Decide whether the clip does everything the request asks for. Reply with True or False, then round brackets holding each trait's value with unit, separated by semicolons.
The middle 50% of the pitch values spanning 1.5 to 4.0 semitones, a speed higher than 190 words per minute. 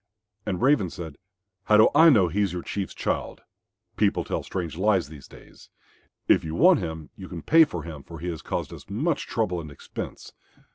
False (4.9 semitones; 200 wpm)